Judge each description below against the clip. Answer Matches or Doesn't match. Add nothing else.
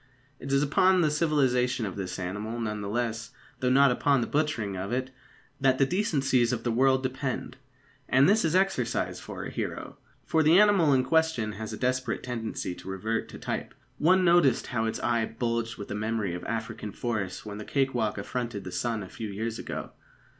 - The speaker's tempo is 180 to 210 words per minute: Matches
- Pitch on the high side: Doesn't match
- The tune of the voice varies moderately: Matches